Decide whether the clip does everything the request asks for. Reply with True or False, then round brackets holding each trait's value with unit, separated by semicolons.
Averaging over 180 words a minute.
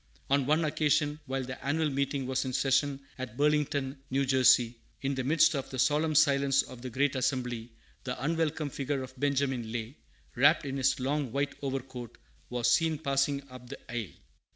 False (175 wpm)